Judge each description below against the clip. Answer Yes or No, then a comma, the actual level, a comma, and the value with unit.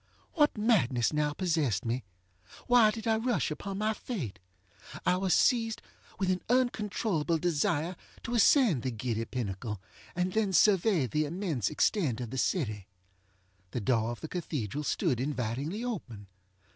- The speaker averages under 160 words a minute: Yes, average, 145 wpm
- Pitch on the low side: No, medium, 160 Hz